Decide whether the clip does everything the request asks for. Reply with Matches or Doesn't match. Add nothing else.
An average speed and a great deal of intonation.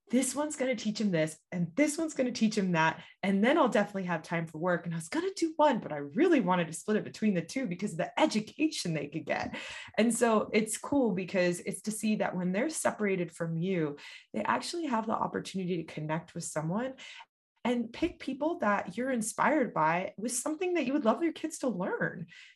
Doesn't match